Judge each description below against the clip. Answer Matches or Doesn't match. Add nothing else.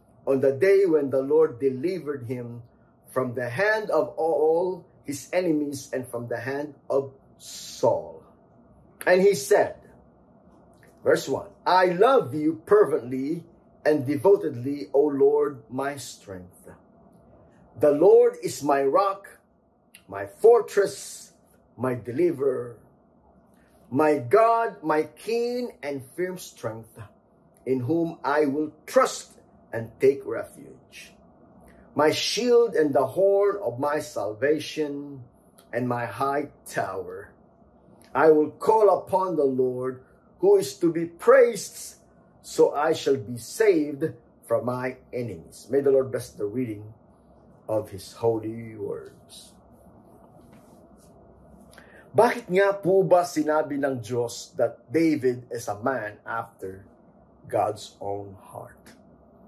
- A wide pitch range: Matches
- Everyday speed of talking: Doesn't match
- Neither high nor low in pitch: Matches